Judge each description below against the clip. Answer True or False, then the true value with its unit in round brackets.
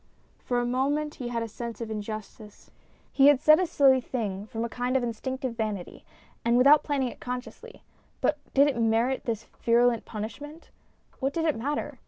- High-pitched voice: True (245 Hz)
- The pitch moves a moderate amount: True (3.3 semitones)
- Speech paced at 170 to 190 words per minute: True (185 wpm)